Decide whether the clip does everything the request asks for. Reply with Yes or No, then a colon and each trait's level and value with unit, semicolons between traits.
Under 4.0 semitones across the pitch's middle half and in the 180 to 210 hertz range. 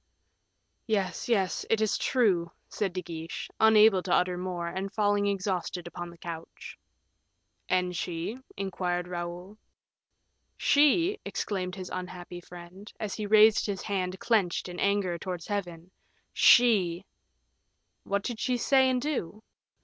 Yes: average, 3.3 semitones; high, 190 Hz